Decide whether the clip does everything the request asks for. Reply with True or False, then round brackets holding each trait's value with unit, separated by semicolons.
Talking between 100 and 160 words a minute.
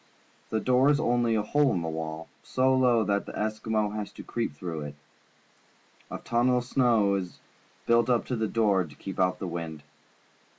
False (195 wpm)